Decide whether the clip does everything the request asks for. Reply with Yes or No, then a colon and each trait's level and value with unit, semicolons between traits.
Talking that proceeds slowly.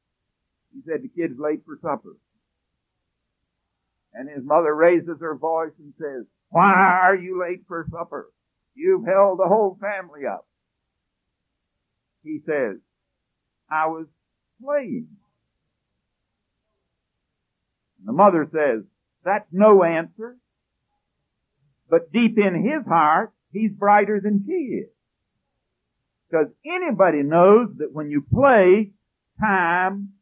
Yes: slow, 115 wpm